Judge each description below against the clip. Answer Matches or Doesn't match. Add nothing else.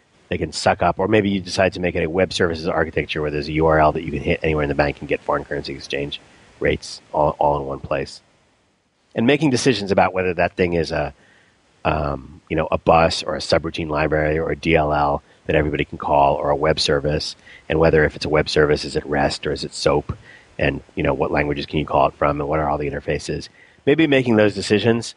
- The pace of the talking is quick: Matches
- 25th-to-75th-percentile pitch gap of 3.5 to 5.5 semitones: Matches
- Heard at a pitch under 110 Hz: Matches